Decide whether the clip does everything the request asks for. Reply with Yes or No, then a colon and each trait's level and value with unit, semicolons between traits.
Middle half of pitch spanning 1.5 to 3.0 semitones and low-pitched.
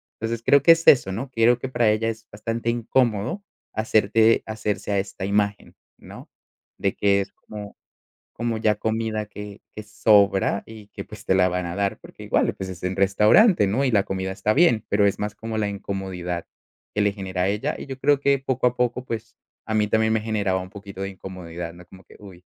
Yes: average, 2.7 semitones; low, 105 Hz